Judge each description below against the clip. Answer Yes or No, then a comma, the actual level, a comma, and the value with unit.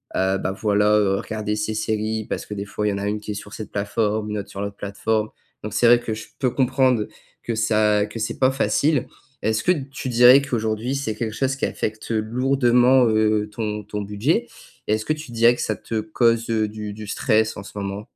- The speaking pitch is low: Yes, low, 110 Hz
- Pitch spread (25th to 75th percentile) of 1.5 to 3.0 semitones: Yes, narrow, 2.4 semitones